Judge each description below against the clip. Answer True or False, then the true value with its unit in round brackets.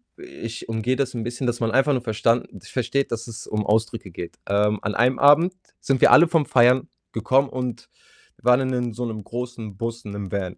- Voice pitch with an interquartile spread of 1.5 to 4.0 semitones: True (2.8 semitones)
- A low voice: True (120 Hz)